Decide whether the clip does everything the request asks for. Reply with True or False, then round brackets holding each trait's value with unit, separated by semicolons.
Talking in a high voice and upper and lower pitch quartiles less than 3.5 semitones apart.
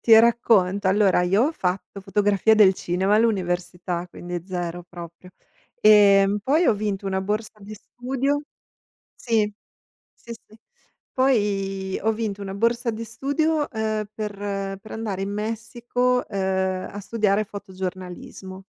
True (205 Hz; 2.9 semitones)